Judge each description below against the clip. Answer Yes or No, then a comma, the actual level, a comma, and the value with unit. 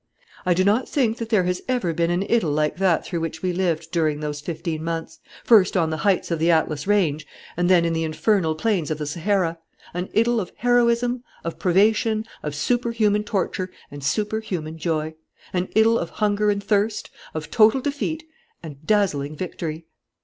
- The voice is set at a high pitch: No, medium, 180 Hz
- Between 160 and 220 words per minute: Yes, average, 185 wpm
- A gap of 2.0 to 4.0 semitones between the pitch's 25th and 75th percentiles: No, average, 5.0 semitones